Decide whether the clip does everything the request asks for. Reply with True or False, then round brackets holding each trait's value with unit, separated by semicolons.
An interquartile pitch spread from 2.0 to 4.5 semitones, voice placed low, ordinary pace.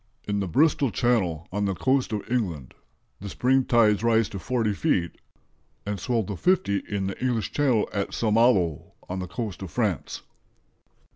True (4.2 semitones; 105 Hz; 170 wpm)